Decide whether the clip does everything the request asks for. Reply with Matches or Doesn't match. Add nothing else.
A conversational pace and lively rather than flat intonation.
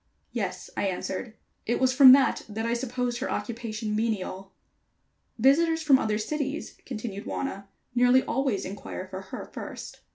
Doesn't match